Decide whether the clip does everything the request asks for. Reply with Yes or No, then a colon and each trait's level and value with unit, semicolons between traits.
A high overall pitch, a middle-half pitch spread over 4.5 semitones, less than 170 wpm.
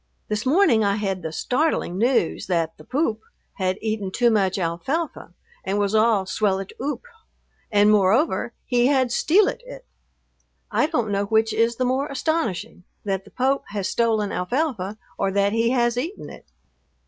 Yes: high, 220 Hz; average, 4.9 semitones; average, 160 wpm